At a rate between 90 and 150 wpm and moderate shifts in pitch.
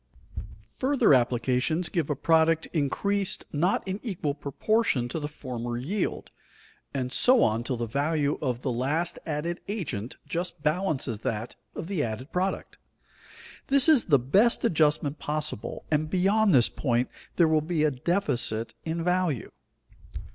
No: average, 145 wpm; wide, 5.8 semitones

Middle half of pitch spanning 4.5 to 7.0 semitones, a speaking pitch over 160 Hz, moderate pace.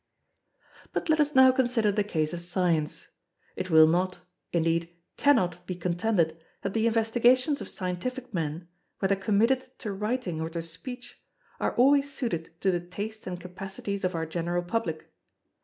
Yes: wide, 5.6 semitones; high, 190 Hz; average, 155 wpm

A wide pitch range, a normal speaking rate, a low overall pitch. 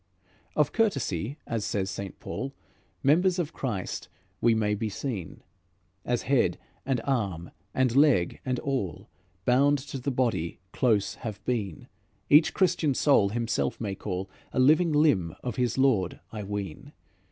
Yes: wide, 5.7 semitones; average, 145 wpm; low, 120 Hz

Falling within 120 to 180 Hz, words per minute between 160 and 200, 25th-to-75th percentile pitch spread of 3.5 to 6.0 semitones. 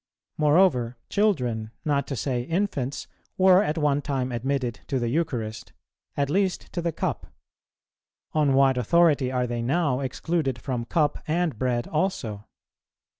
No: medium, 140 Hz; average, 140 wpm; average, 4.9 semitones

